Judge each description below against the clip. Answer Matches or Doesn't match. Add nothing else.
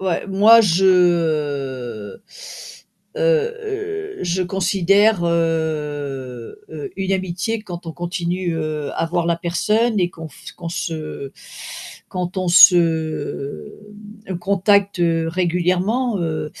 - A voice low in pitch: Doesn't match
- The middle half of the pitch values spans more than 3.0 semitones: Matches